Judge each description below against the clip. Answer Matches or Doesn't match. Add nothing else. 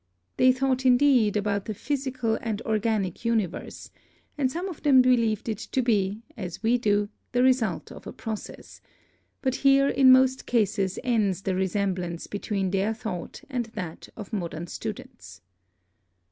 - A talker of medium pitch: Doesn't match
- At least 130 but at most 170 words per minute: Matches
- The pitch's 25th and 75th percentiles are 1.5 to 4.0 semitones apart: Doesn't match